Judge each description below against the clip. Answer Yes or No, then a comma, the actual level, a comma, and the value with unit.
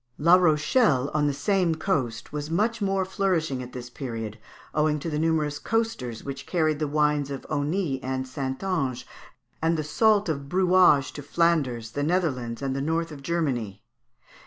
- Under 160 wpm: No, average, 165 wpm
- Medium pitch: Yes, medium, 150 Hz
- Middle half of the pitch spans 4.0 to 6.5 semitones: Yes, average, 4.3 semitones